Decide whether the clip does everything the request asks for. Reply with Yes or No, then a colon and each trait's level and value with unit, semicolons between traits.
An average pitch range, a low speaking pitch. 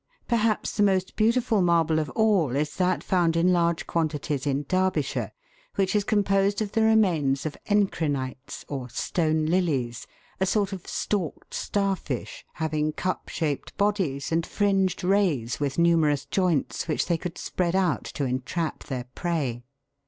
No: average, 4.8 semitones; medium, 170 Hz